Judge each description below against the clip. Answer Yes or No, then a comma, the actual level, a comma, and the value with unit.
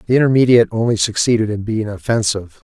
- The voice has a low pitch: Yes, low, 110 Hz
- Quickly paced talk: No, average, 155 wpm